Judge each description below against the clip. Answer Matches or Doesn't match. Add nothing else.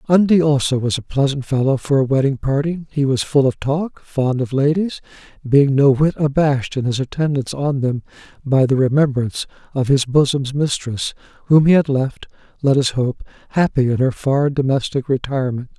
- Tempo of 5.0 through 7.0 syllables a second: Matches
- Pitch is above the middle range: Doesn't match